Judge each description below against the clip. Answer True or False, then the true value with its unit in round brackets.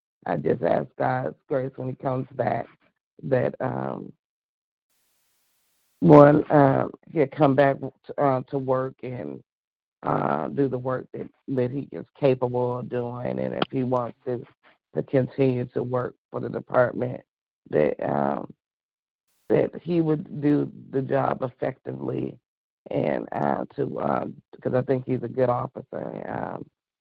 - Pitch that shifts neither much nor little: False (1.9 semitones)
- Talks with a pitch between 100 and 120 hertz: False (130 Hz)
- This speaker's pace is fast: False (145 wpm)